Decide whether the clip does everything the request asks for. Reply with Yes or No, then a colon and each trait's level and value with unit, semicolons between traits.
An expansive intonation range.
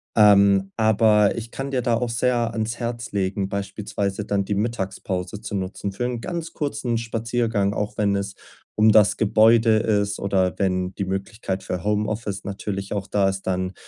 No: average, 2.7 semitones